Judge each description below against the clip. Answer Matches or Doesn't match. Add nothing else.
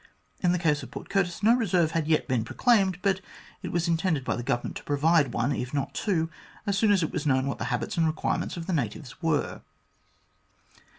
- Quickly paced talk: Matches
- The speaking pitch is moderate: Matches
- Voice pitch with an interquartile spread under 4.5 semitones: Doesn't match